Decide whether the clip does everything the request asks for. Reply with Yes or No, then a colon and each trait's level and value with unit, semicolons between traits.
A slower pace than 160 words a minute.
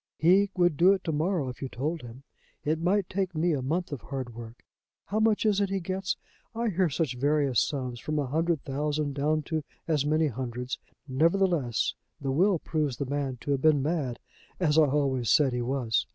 No: fast, 205 wpm